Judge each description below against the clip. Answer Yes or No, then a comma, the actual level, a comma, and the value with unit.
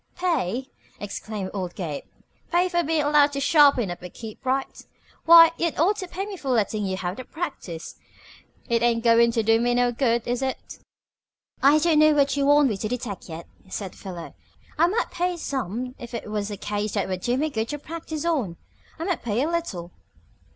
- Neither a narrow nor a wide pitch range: No, wide, 6.6 semitones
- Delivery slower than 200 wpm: No, fast, 205 wpm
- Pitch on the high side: Yes, very high, 250 Hz